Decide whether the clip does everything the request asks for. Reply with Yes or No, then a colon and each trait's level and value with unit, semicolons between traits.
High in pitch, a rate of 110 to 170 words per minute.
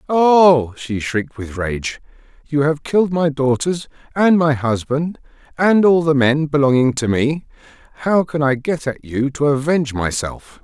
No: medium, 140 Hz; average, 165 wpm